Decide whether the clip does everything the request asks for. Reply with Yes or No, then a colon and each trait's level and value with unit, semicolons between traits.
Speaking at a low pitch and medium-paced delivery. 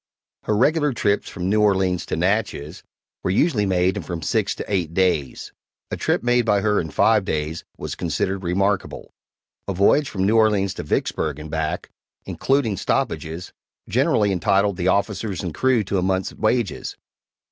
Yes: very low, 95 Hz; average, 170 wpm